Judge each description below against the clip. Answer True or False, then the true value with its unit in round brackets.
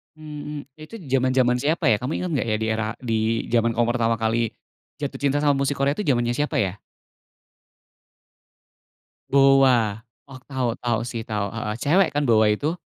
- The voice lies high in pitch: False (125 Hz)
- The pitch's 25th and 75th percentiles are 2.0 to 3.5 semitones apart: False (3.9 semitones)